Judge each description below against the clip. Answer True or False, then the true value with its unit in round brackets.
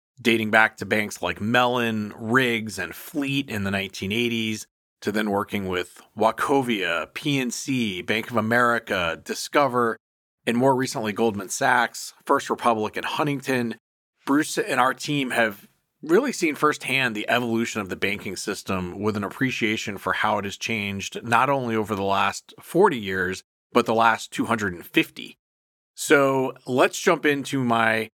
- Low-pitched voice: True (115 Hz)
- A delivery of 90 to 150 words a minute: True (145 wpm)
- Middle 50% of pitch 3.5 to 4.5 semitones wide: True (3.8 semitones)